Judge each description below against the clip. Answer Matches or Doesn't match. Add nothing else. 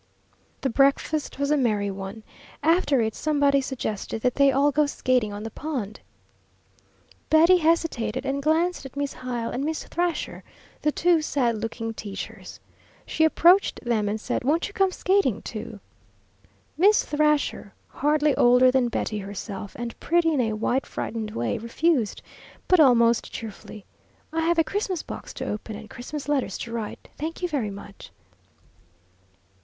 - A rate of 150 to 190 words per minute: Matches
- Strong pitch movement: Matches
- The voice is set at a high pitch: Matches